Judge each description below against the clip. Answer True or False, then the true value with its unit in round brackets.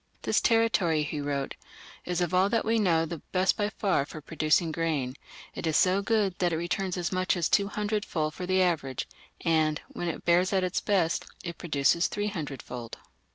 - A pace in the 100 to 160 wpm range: False (195 wpm)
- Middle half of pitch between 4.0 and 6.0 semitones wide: False (3.6 semitones)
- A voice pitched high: False (175 Hz)